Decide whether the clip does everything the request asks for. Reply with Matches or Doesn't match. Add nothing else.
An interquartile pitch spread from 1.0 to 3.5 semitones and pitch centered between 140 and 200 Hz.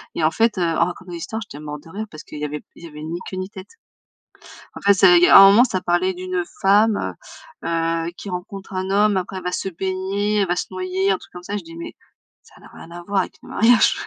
Matches